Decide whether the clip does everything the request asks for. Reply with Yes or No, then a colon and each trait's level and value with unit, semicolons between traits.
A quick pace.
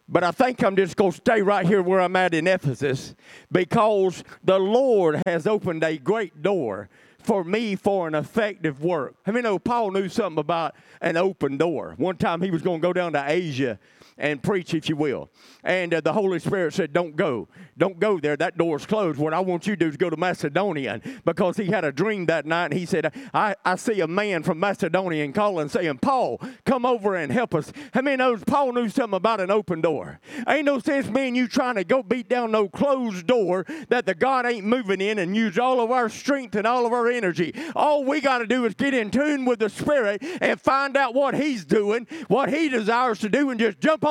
Yes: fast, 230 wpm